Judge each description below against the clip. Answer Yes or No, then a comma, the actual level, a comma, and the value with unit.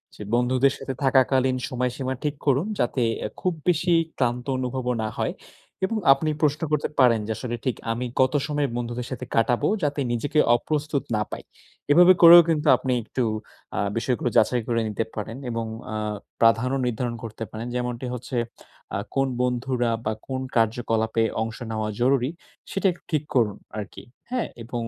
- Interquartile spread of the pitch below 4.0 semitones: Yes, average, 2.9 semitones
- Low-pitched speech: Yes, low, 125 Hz